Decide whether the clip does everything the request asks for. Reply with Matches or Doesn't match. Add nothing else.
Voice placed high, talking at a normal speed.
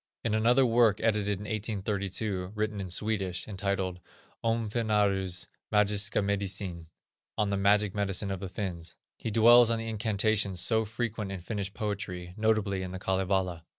Doesn't match